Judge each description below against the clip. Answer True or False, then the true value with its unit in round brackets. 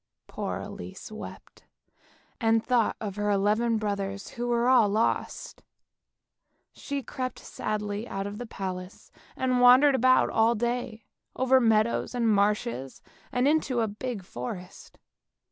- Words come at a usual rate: False (130 wpm)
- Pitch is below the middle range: False (225 Hz)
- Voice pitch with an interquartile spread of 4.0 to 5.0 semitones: False (3.4 semitones)